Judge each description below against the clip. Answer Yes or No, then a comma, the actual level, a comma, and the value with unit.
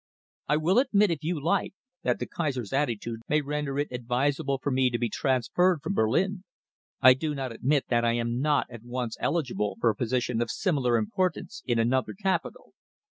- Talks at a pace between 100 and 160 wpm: No, average, 190 wpm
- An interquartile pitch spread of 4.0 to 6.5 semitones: Yes, average, 4.6 semitones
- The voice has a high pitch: No, low, 135 Hz